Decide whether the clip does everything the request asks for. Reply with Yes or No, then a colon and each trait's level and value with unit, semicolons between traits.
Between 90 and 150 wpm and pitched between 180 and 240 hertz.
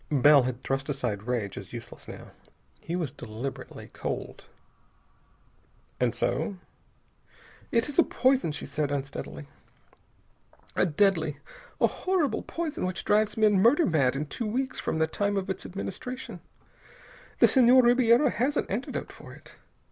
Yes: average, 145 wpm; medium, 185 Hz